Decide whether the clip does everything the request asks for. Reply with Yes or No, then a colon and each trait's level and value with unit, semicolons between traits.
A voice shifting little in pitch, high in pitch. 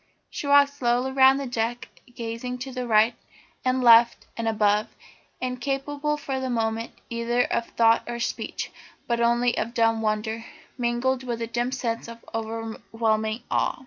Yes: narrow, 2.0 semitones; high, 235 Hz